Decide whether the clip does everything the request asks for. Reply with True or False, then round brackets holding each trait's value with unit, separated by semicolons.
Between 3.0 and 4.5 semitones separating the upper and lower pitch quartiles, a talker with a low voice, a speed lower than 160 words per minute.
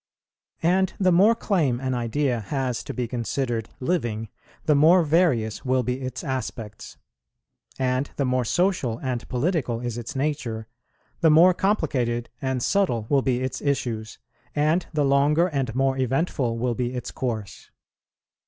True (4.1 semitones; 130 Hz; 150 wpm)